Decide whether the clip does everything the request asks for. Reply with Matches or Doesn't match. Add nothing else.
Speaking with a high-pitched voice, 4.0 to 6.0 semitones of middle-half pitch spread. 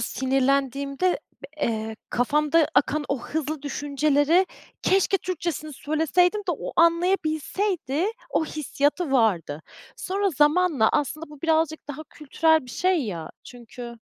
Doesn't match